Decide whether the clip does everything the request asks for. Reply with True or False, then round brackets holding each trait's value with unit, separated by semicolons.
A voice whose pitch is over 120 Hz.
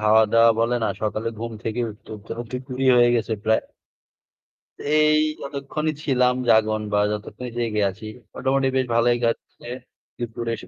False (115 Hz)